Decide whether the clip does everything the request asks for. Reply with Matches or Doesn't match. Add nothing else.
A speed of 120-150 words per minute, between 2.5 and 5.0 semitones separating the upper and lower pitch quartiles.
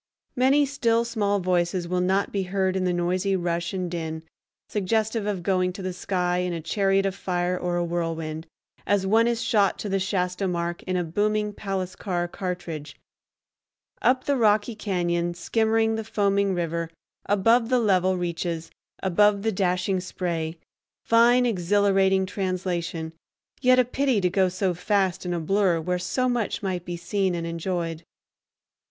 Doesn't match